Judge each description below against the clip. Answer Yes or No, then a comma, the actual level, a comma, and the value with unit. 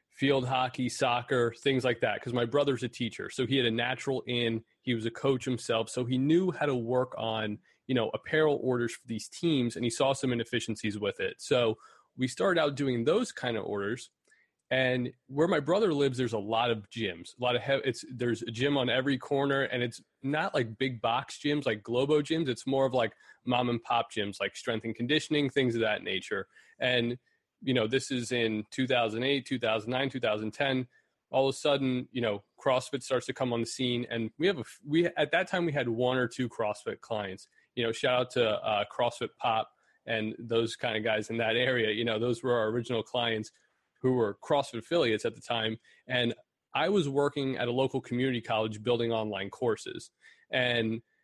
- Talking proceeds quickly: Yes, fast, 210 wpm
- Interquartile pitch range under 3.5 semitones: Yes, average, 2.8 semitones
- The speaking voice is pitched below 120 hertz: No, low, 125 Hz